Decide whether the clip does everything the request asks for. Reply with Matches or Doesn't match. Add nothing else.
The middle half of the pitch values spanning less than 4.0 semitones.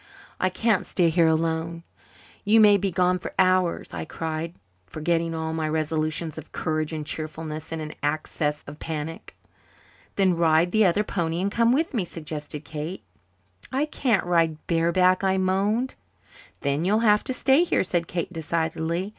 Matches